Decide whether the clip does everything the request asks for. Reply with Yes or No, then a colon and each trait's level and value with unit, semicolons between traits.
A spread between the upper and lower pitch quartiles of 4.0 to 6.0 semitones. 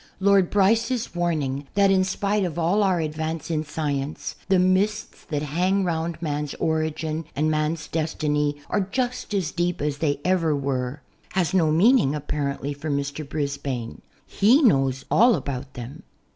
Yes: average, 4.5 semitones